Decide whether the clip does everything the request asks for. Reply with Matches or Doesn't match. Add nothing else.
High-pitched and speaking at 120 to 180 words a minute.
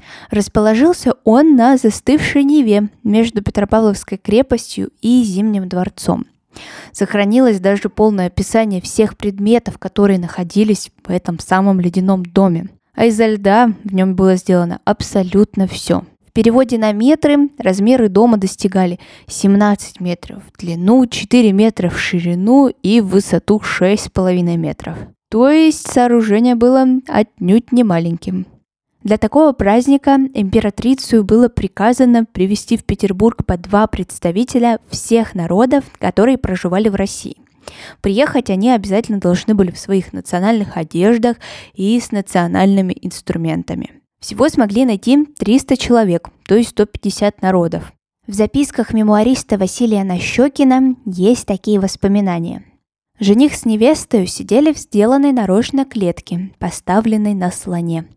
Matches